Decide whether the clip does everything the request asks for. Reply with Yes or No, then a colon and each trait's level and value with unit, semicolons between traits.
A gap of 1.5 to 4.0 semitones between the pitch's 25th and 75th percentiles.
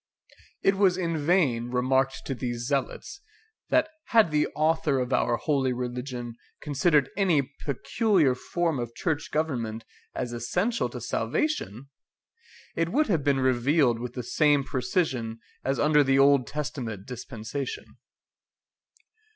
No: average, 4.5 semitones